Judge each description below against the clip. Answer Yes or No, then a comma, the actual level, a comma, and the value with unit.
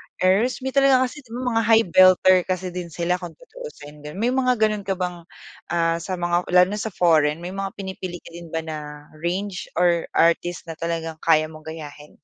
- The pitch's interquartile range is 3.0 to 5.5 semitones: Yes, average, 3.8 semitones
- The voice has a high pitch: No, medium, 180 Hz